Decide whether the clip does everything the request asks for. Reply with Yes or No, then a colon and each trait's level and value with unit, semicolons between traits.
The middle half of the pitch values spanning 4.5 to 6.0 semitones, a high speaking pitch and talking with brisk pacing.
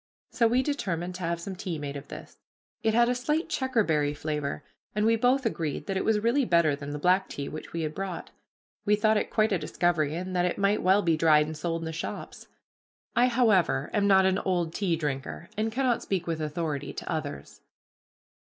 No: wide, 5.6 semitones; medium, 180 Hz; fast, 220 wpm